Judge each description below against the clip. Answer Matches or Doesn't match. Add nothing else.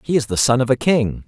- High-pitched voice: Doesn't match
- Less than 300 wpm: Doesn't match